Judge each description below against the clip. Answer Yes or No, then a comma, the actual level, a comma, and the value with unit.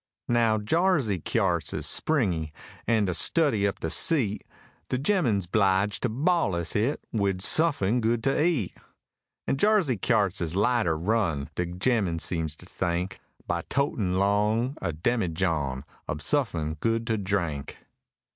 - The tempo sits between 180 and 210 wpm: No, average, 140 wpm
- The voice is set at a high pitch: No, low, 105 Hz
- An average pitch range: No, wide, 5.9 semitones